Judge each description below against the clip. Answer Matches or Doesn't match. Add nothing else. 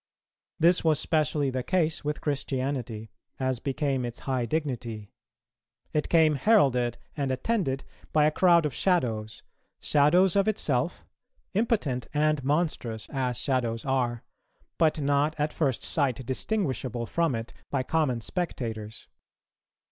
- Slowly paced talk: Matches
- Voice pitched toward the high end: Doesn't match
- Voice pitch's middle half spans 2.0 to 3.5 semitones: Doesn't match